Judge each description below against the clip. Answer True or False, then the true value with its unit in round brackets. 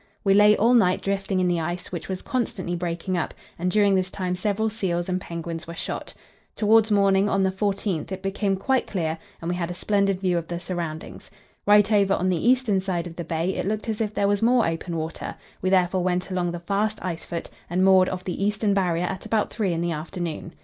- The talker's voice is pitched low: False (185 Hz)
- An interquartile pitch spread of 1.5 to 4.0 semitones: True (2.7 semitones)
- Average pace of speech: False (230 wpm)